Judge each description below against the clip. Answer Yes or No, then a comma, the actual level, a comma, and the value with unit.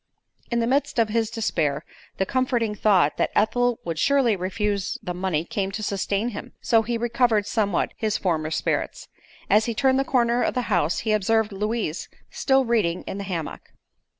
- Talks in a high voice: Yes, high, 215 Hz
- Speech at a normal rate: Yes, average, 180 wpm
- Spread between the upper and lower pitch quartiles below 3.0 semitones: No, average, 3.7 semitones